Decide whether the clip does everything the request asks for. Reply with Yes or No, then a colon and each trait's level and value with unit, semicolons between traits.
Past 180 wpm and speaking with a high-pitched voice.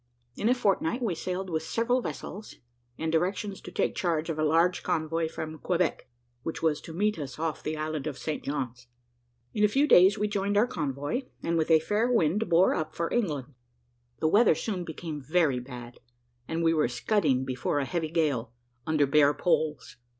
No: average, 190 wpm; medium, 160 Hz